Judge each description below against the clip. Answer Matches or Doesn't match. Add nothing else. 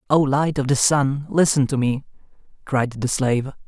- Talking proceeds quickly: Doesn't match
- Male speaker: Matches